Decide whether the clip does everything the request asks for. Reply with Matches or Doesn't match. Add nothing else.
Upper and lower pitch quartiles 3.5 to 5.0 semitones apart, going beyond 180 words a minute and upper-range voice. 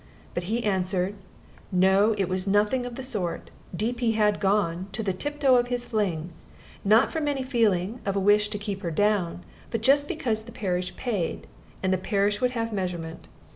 Matches